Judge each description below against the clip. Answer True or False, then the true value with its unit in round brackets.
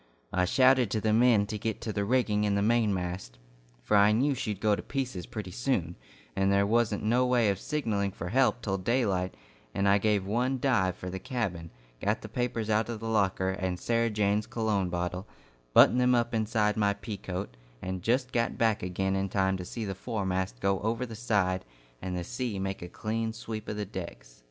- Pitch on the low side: True (105 Hz)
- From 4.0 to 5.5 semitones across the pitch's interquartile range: False (3.5 semitones)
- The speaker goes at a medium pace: False (210 wpm)